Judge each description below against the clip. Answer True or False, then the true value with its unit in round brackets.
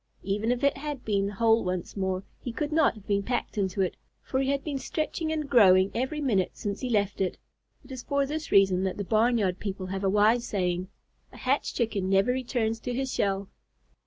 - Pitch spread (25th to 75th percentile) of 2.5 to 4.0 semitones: False (5.2 semitones)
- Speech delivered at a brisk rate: True (220 wpm)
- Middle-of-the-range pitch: False (220 Hz)